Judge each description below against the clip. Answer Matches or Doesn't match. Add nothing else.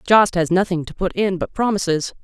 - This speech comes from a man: Doesn't match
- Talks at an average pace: Doesn't match